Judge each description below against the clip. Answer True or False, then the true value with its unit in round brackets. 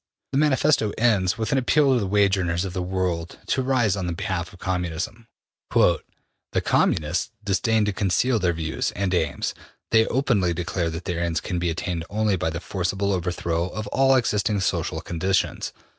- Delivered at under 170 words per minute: False (175 wpm)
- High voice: False (95 Hz)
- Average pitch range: True (3.9 semitones)